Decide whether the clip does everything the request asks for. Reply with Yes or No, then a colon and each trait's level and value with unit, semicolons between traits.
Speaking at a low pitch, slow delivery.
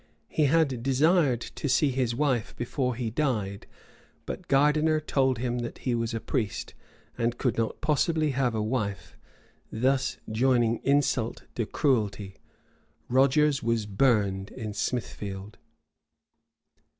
Yes: low, 125 Hz; slow, 125 wpm